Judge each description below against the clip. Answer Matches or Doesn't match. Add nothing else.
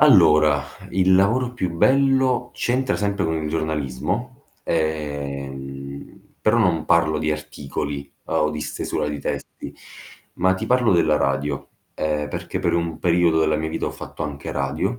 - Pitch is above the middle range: Doesn't match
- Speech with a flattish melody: Doesn't match